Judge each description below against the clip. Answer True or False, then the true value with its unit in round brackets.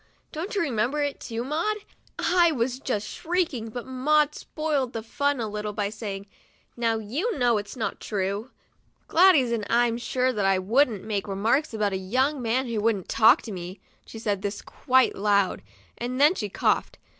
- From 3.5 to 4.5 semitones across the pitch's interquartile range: False (5.1 semitones)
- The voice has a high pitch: True (235 Hz)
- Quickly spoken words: False (190 wpm)